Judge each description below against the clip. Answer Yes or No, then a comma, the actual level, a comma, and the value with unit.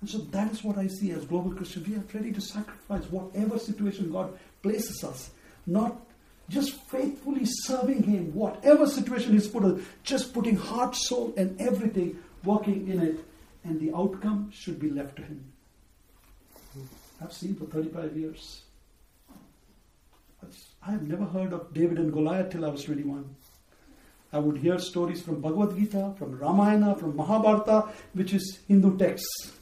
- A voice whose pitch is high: Yes, high, 195 Hz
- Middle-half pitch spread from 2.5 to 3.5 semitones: No, average, 4.6 semitones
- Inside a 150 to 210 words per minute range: Yes, average, 160 wpm